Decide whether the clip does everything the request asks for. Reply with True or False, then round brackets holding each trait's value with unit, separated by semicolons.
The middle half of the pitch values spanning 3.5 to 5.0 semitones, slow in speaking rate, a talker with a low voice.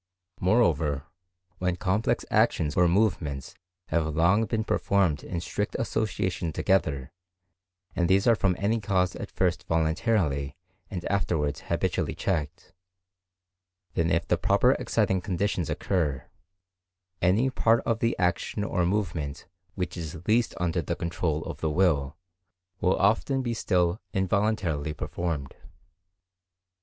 True (4.1 semitones; 125 wpm; 90 Hz)